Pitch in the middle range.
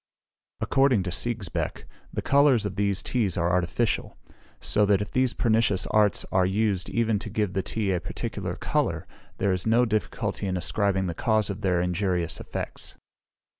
No: low, 100 Hz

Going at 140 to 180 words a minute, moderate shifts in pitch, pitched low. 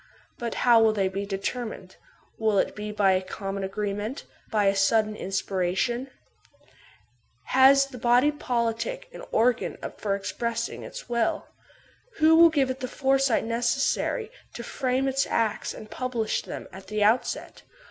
No: average, 150 wpm; average, 4.1 semitones; high, 230 Hz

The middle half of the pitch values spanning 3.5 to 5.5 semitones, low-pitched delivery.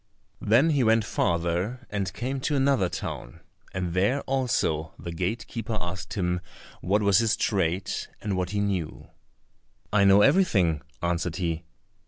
Yes: average, 4.8 semitones; low, 100 Hz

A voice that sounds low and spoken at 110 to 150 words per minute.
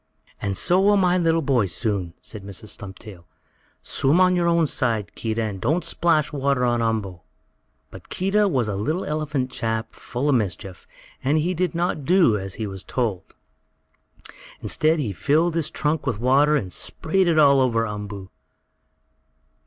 No: low, 130 Hz; average, 165 wpm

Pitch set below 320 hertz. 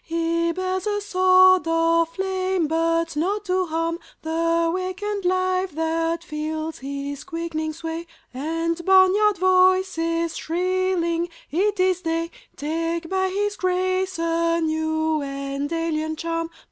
No: very high, 335 Hz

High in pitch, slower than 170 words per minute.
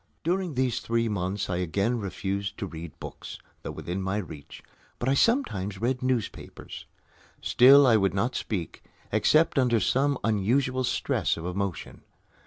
No: low, 110 Hz; average, 150 wpm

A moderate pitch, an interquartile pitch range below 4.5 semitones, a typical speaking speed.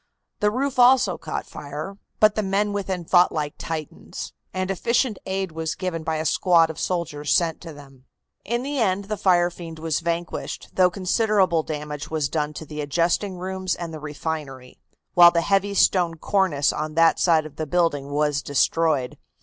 Yes: medium, 170 Hz; average, 3.7 semitones; average, 180 wpm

